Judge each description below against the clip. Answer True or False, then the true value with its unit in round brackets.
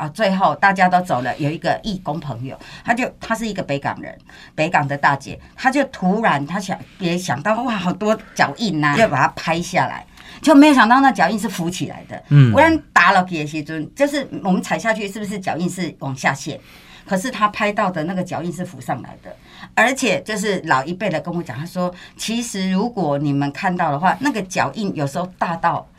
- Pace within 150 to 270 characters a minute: False (310 characters per minute)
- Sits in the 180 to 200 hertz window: True (185 Hz)